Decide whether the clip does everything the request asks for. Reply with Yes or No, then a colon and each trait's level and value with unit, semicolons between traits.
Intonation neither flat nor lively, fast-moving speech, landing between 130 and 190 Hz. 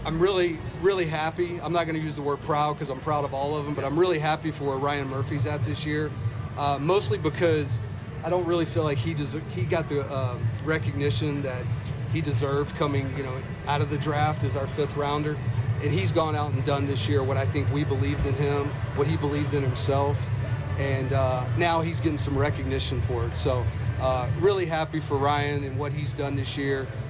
Yes: average, 3.4 semitones; fast, 220 wpm; medium, 140 Hz